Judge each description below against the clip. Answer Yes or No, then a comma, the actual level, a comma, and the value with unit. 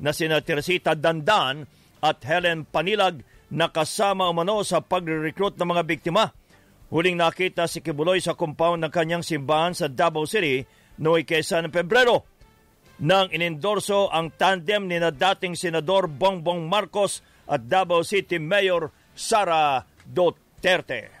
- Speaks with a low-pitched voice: No, medium, 170 Hz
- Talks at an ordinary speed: No, slow, 125 wpm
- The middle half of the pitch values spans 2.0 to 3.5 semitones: Yes, average, 2.9 semitones